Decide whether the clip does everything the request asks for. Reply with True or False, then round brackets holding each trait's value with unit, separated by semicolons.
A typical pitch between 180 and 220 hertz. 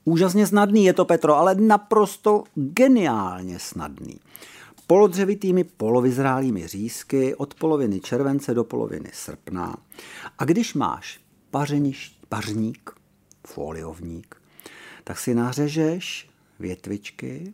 False (140 Hz)